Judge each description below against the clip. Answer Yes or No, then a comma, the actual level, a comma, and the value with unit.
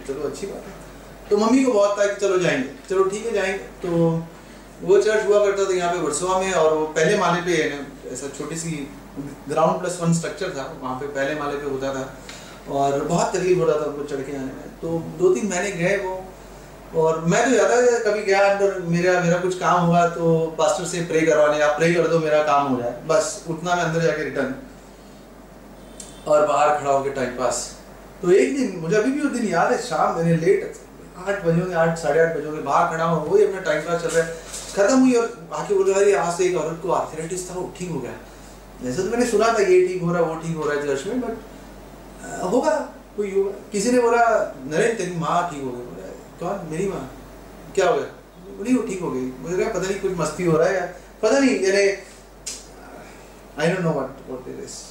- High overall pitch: No, medium, 175 Hz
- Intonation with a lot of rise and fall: No, average, 4.4 semitones